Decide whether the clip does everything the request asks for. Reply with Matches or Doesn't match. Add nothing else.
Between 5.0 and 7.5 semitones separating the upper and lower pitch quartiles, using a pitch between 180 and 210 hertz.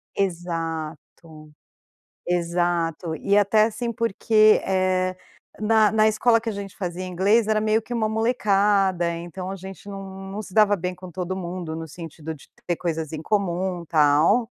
Doesn't match